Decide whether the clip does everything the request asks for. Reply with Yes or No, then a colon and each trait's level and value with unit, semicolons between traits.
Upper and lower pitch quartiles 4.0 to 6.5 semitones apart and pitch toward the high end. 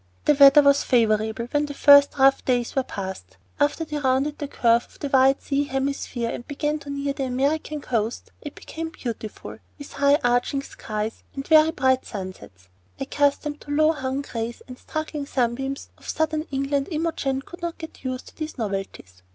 No: average, 3.2 semitones; very high, 275 Hz